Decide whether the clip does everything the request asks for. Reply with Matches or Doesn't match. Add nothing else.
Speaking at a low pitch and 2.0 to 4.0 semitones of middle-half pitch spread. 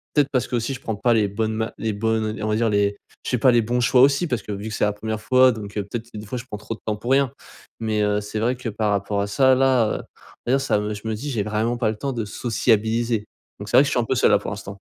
Matches